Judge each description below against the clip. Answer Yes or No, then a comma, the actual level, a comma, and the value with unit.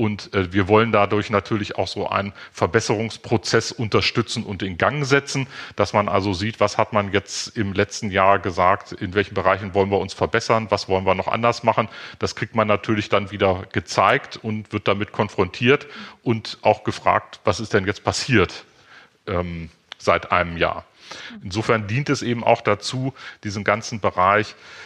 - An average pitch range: No, narrow, 2.2 semitones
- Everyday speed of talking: Yes, average, 170 wpm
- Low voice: Yes, low, 105 Hz